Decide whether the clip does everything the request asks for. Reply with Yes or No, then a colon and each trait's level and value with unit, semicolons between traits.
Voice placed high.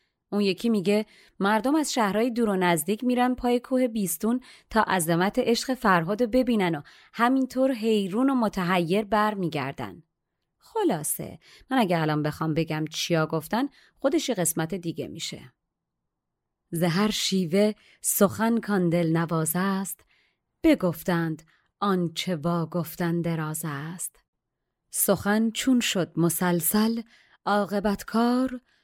Yes: high, 200 Hz